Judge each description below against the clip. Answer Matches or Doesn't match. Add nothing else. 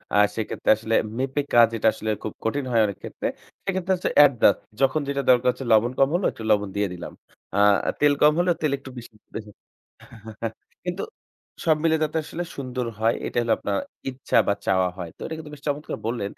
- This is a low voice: Matches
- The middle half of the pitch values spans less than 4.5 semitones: Doesn't match